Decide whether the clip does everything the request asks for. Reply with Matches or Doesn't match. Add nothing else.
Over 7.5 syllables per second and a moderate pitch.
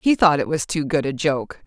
Doesn't match